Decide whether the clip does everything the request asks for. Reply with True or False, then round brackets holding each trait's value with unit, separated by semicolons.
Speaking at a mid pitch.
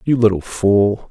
False (105 Hz)